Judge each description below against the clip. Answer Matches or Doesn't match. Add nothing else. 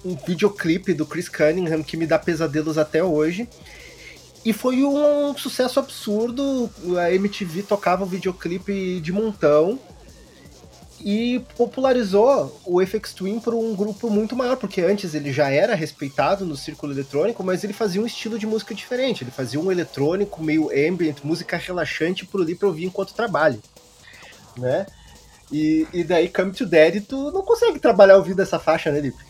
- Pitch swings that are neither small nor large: Doesn't match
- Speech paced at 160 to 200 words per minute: Matches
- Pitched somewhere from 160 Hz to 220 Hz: Matches